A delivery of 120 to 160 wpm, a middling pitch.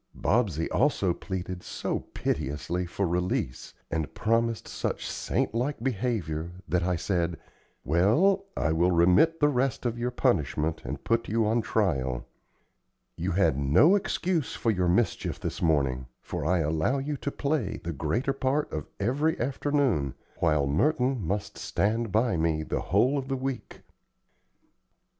No: average, 150 wpm; low, 100 Hz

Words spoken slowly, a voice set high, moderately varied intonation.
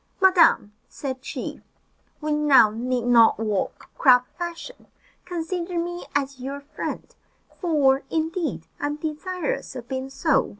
Yes: slow, 130 wpm; very high, 290 Hz; average, 4.6 semitones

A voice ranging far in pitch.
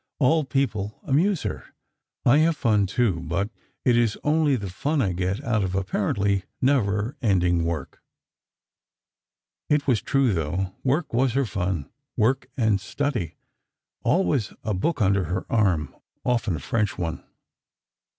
Yes: wide, 6.2 semitones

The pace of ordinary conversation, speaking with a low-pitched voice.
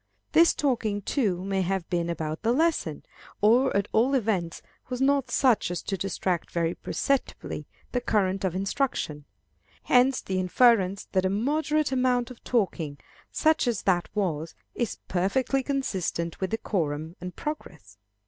No: average, 150 wpm; high, 200 Hz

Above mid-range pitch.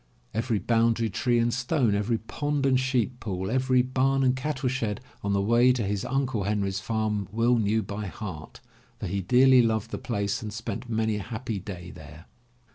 No: low, 115 Hz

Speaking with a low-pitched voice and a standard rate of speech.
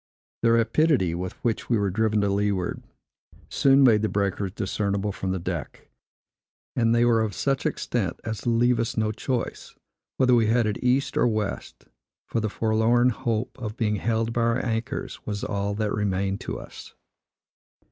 Yes: low, 110 Hz; average, 165 wpm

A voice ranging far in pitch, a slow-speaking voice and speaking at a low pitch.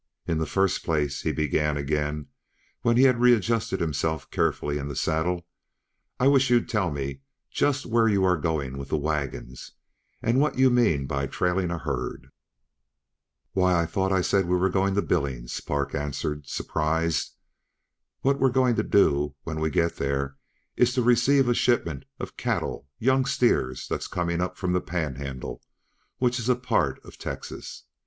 No: wide, 8.3 semitones; average, 170 wpm; very low, 85 Hz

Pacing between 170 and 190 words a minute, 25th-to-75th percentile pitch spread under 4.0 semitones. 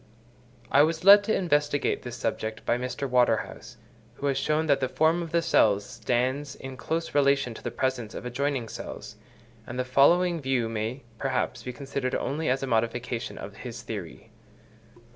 Yes: average, 175 wpm; average, 3.1 semitones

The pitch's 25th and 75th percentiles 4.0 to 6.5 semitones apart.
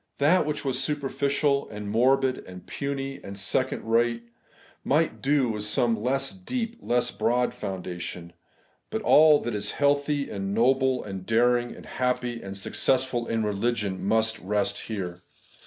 Yes: average, 4.7 semitones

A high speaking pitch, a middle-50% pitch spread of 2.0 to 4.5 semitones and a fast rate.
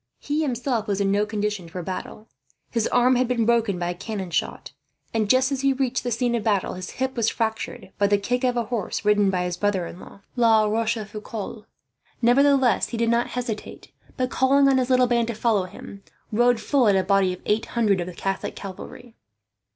Yes: high, 225 Hz; average, 3.5 semitones; fast, 215 wpm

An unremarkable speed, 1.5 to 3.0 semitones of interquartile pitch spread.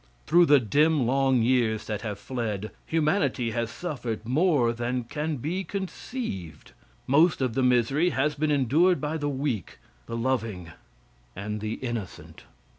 No: average, 145 wpm; average, 4.9 semitones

